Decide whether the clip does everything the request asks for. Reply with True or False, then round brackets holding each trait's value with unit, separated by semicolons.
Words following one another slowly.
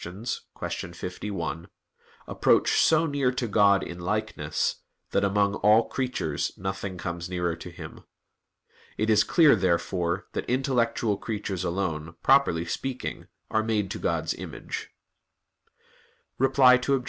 True (120 wpm)